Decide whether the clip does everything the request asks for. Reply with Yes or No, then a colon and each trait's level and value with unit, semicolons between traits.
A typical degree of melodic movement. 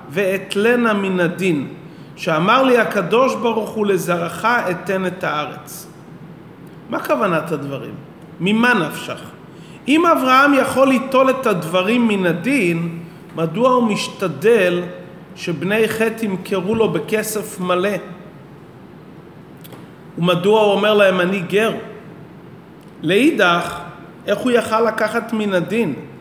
Yes: average, 4.2 semitones